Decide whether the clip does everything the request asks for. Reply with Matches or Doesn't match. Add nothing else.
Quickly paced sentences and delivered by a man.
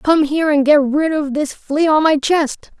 Doesn't match